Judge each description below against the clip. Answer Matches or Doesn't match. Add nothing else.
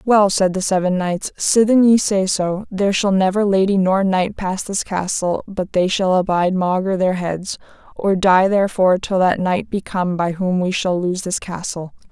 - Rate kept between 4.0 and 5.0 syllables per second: Matches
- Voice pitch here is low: Doesn't match